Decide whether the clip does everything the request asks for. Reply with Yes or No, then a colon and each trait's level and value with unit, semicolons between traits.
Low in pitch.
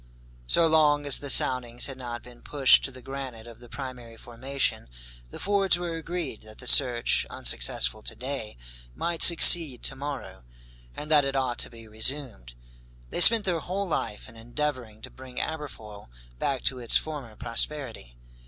Yes: low, 130 Hz